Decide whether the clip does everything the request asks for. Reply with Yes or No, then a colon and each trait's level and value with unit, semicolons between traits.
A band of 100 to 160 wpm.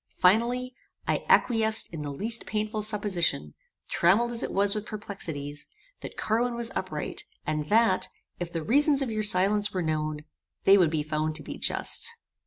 No: average, 170 wpm